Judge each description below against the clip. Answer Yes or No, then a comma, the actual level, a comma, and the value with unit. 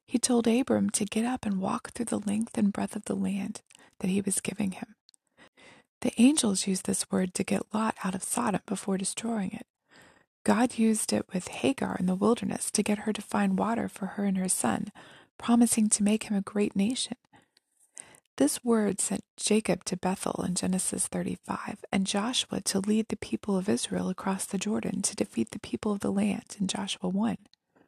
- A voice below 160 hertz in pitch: No, high, 210 Hz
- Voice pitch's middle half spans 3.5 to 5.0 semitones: No, average, 2.8 semitones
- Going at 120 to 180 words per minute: No, average, 195 wpm